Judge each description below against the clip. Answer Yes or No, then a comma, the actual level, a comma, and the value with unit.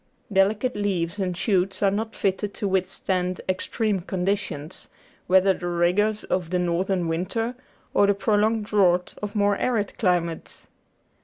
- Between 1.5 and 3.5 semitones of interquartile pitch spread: Yes, narrow, 2.4 semitones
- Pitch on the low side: No, high, 195 Hz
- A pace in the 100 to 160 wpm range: Yes, average, 140 wpm